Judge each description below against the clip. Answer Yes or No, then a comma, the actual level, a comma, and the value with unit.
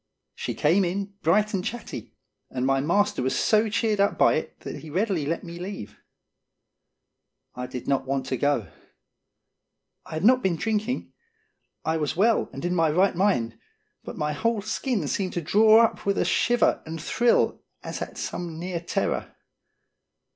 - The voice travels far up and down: Yes, wide, 5.9 semitones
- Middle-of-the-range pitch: Yes, medium, 180 Hz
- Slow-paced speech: No, average, 175 wpm